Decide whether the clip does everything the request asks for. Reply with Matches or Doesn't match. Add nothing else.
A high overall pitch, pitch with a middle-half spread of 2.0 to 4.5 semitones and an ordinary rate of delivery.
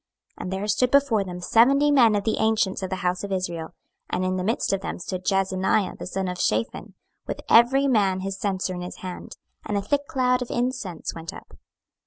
Doesn't match